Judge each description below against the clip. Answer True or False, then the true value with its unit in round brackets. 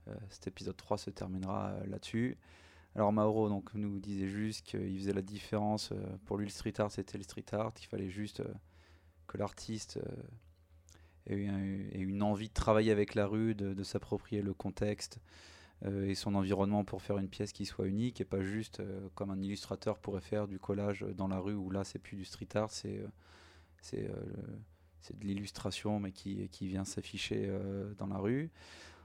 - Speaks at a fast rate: False (195 wpm)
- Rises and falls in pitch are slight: True (1.8 semitones)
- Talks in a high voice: False (100 Hz)